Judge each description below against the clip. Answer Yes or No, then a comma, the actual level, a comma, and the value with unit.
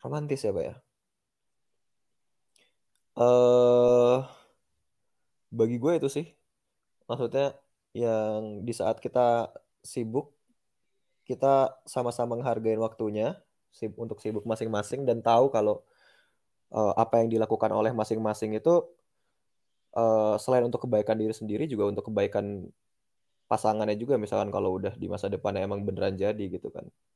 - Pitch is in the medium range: No, low, 115 Hz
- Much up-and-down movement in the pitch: No, narrow, 2.6 semitones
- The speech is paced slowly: No, average, 120 wpm